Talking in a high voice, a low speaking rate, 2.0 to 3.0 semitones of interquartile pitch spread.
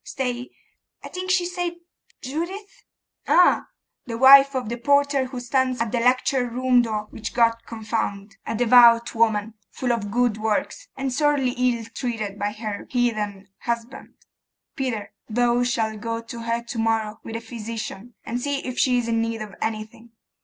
No: high, 235 Hz; average, 165 wpm; narrow, 2.5 semitones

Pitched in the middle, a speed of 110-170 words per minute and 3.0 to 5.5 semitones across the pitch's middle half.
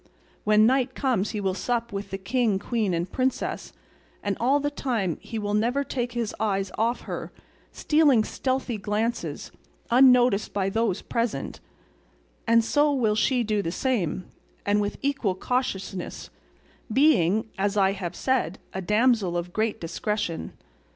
No: high, 220 Hz; average, 145 wpm; average, 4.2 semitones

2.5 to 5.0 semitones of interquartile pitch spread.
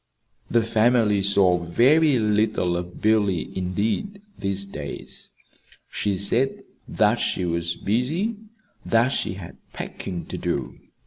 Yes: average, 4.6 semitones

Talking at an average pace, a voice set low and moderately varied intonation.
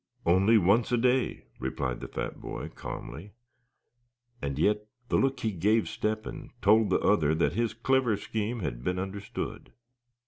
Yes: average, 160 wpm; low, 105 Hz; average, 4.1 semitones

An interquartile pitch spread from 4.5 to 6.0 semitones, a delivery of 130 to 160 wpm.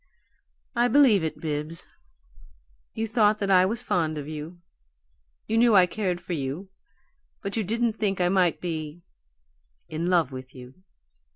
Yes: average, 5.3 semitones; average, 155 wpm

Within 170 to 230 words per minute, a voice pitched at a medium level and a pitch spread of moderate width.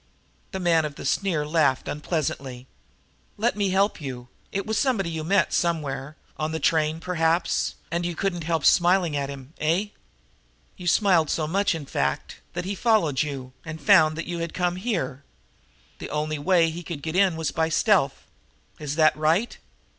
Yes: average, 175 wpm; medium, 165 Hz; average, 3.3 semitones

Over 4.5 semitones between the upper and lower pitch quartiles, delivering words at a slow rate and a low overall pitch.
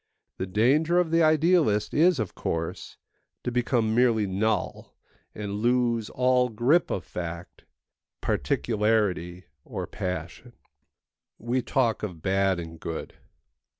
Yes: average, 5.1 semitones; slow, 115 wpm; low, 110 Hz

